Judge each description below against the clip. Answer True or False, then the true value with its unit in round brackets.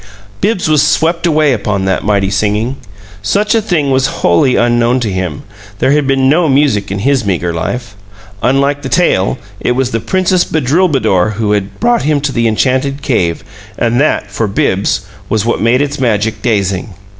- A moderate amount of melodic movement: False (5.7 semitones)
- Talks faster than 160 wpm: True (180 wpm)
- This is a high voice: False (125 Hz)